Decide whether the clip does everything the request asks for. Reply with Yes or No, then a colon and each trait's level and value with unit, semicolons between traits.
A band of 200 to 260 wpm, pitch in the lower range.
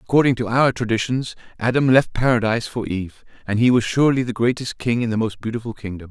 Yes: fast, 205 wpm; low, 115 Hz